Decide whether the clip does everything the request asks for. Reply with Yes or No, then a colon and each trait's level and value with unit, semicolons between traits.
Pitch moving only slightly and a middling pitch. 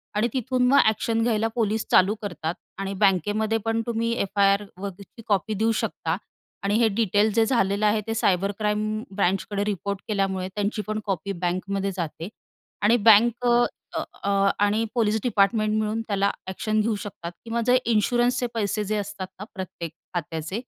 No: narrow, 2.2 semitones; high, 210 Hz